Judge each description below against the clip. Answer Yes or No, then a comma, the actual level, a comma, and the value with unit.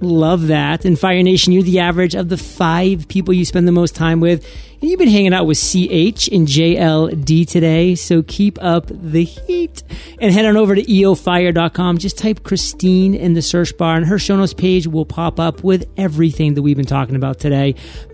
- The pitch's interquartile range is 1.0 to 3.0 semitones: Yes, narrow, 2.4 semitones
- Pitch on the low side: No, medium, 175 Hz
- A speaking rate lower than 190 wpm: No, fast, 205 wpm